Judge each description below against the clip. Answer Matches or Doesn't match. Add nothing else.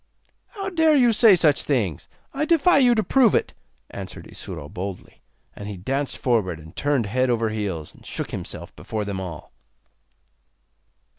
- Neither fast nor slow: Matches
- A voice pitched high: Doesn't match